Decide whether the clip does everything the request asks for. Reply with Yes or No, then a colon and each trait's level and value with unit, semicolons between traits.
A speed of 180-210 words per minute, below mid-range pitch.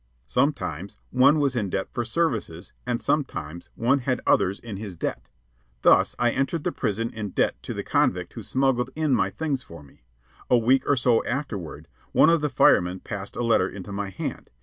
Yes: average, 195 wpm; low, 115 Hz